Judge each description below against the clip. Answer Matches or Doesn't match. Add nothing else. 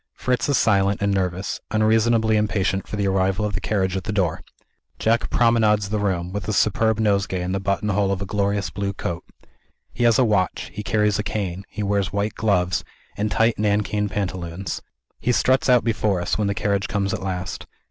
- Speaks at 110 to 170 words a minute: Doesn't match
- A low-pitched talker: Matches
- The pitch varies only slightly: Matches